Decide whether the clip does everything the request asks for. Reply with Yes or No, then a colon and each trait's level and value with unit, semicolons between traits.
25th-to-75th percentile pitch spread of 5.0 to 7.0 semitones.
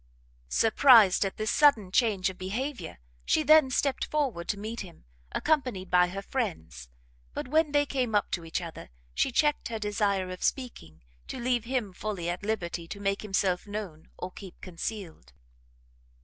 Yes: wide, 5.6 semitones